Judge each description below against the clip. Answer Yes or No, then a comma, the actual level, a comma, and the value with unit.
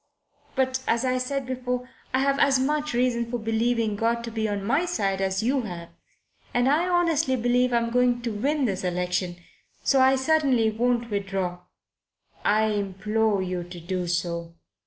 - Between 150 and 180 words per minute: Yes, average, 165 wpm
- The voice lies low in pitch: No, high, 235 Hz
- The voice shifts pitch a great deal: No, average, 4.8 semitones